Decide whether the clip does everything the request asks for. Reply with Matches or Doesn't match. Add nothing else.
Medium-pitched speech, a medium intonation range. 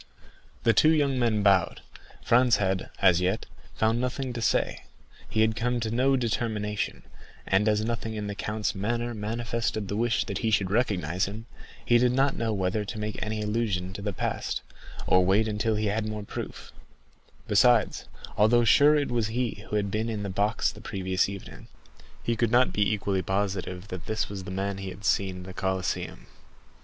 Doesn't match